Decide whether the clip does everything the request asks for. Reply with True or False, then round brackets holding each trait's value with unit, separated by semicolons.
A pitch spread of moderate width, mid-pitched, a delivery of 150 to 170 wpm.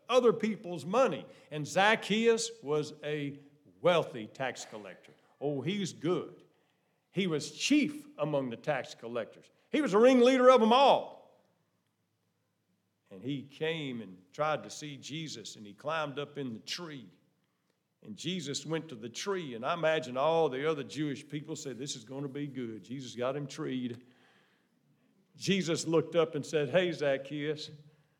True (4.0 semitones; 150 Hz; 155 wpm)